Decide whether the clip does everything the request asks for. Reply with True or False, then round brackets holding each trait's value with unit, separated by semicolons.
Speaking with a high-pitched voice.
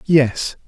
False (140 Hz)